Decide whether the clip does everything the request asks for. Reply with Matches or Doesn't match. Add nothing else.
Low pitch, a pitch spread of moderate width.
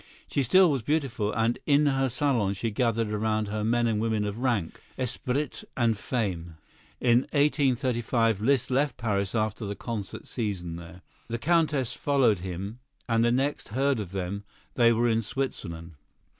Matches